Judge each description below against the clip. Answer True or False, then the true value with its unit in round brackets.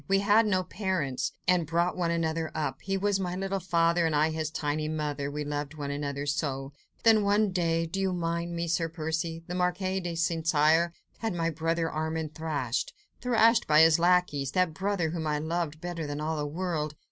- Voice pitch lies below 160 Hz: False (165 Hz)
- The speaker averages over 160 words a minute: True (190 wpm)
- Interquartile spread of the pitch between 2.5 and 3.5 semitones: True (2.8 semitones)